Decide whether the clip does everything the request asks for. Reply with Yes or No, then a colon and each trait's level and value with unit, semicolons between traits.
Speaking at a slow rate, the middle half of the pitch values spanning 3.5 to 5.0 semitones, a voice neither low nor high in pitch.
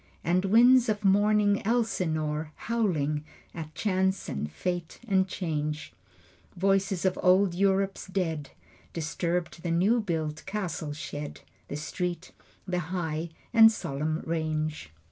Yes: slow, 120 wpm; average, 3.9 semitones; medium, 180 Hz